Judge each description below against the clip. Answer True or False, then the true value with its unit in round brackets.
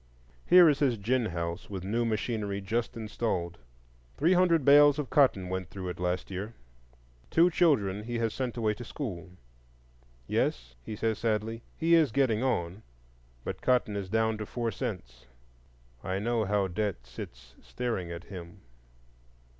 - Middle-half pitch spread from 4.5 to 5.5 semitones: True (4.8 semitones)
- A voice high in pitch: False (110 Hz)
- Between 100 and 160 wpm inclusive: True (155 wpm)